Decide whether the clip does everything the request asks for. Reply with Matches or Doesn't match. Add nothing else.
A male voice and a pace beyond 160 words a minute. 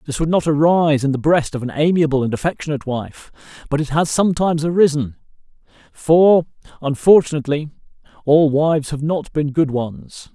Doesn't match